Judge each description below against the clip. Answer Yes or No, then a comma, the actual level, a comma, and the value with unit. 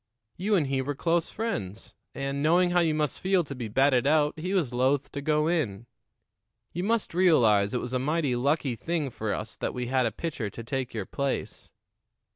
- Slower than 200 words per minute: No, fast, 205 wpm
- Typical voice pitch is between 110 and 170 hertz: Yes, medium, 140 Hz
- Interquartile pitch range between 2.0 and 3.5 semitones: No, average, 5.1 semitones